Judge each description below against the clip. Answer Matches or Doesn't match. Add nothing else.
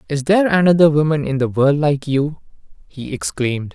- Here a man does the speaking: Matches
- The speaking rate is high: Doesn't match